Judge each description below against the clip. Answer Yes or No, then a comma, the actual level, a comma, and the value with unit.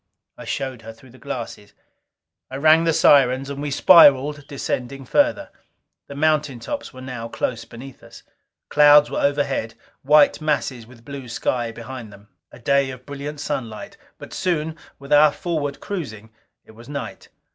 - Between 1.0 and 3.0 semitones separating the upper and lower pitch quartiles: No, average, 3.4 semitones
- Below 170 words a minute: Yes, average, 160 wpm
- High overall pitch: No, medium, 140 Hz